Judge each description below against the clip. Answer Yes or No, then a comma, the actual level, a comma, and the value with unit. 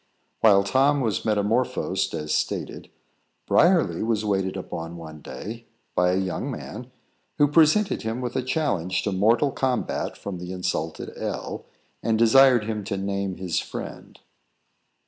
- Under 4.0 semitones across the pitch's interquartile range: No, wide, 5.4 semitones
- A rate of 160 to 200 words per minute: No, average, 145 wpm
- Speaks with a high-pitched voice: No, low, 105 Hz